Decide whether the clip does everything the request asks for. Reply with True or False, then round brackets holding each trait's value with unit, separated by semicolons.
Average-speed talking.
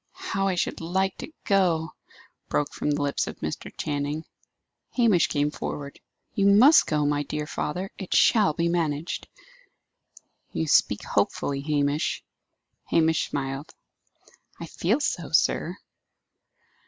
False (130 wpm)